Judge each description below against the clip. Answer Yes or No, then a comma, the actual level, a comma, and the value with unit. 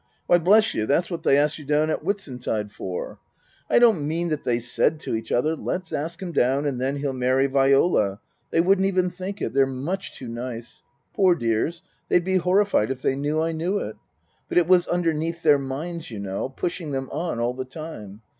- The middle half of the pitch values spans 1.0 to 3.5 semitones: No, average, 5.3 semitones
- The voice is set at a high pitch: No, medium, 150 Hz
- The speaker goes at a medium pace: No, fast, 210 wpm